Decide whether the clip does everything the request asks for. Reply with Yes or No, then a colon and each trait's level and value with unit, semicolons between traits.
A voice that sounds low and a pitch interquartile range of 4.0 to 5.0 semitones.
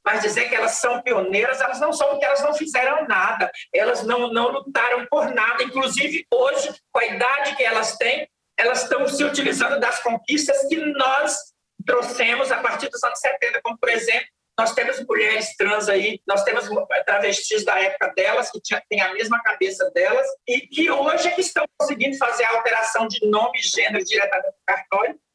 No: very high, 260 Hz; average, 4.4 semitones